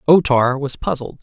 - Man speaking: Yes, male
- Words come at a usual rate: Yes, average, 195 wpm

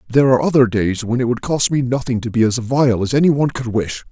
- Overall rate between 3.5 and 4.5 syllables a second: No, 6.2 syllables/s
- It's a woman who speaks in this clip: No, male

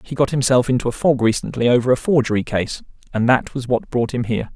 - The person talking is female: No, male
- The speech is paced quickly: Yes, fast, 235 wpm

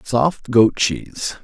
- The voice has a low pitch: Yes, low, 120 Hz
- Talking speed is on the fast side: No, slow, 125 wpm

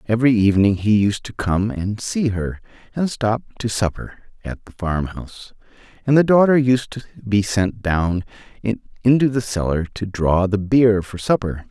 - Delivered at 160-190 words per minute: Yes, average, 170 wpm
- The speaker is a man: Yes, male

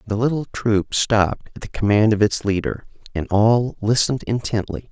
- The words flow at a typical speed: Yes, average, 170 wpm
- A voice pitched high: No, low, 110 Hz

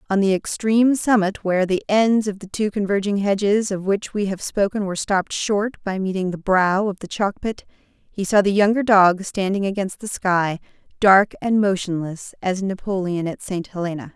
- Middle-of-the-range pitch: No, high, 200 Hz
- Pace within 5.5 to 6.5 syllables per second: No, 4.9 syllables/s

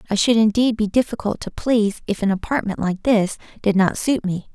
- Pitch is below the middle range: No, high, 215 Hz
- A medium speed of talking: No, fast, 210 wpm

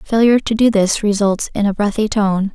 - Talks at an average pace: No, fast, 210 wpm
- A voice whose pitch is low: No, high, 210 Hz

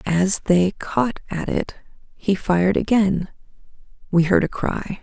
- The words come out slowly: Yes, slow, 130 wpm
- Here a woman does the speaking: Yes, female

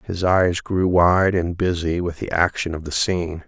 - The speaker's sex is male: Yes, male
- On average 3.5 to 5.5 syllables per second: Yes, 4.5 syllables/s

